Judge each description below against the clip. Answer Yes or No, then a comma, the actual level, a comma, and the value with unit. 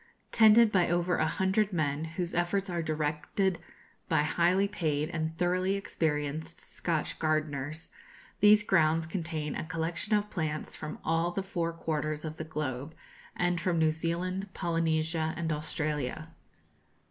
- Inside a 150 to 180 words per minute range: No, average, 140 wpm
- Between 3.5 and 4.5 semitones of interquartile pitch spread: No, narrow, 2.4 semitones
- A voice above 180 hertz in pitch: No, medium, 165 Hz